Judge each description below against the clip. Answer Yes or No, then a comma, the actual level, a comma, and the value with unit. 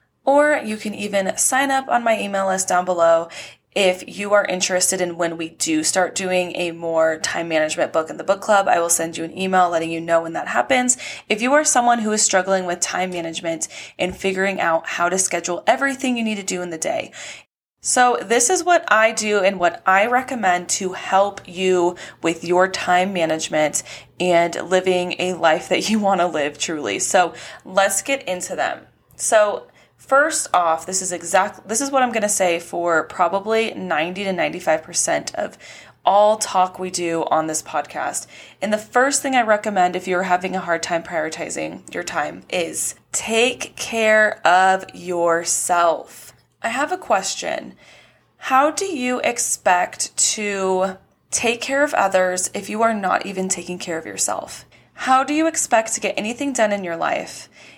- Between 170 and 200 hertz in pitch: Yes, high, 190 Hz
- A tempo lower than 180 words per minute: No, average, 185 wpm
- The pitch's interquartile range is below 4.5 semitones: Yes, average, 4.1 semitones